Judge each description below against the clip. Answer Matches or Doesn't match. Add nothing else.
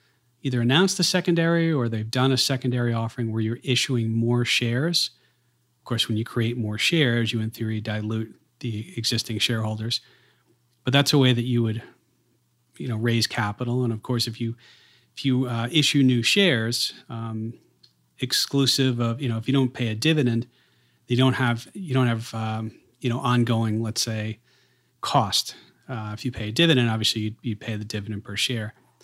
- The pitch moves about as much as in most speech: Doesn't match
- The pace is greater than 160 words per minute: Matches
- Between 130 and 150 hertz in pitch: Doesn't match